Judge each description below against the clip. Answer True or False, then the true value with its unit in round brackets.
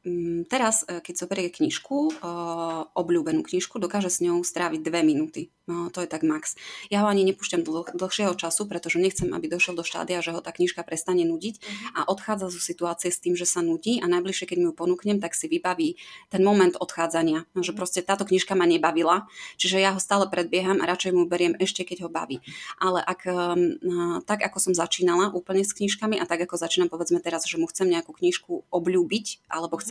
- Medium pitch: True (180 Hz)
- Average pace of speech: False (205 wpm)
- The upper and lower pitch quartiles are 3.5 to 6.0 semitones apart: False (2.8 semitones)